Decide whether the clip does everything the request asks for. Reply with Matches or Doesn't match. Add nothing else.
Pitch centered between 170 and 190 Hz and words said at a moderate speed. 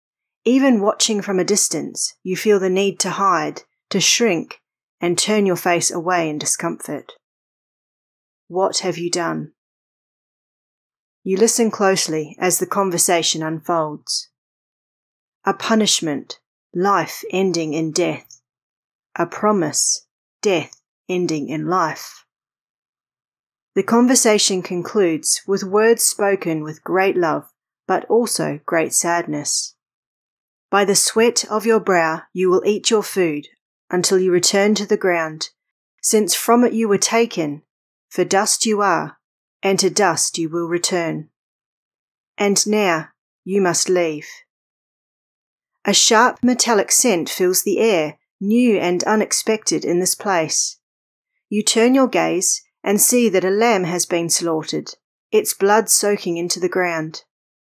Doesn't match